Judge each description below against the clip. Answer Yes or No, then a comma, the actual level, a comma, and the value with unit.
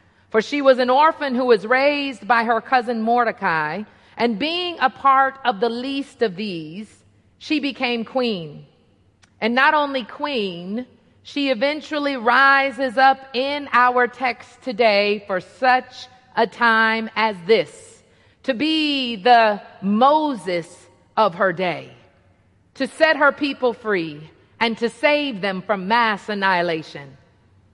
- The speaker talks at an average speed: No, slow, 130 wpm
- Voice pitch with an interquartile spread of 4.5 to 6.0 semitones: Yes, average, 4.8 semitones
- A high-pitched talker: Yes, high, 235 Hz